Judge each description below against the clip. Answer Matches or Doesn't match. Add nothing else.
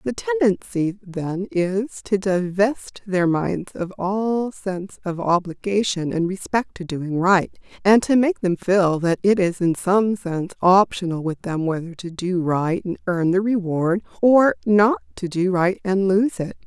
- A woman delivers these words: Matches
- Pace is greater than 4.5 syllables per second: Doesn't match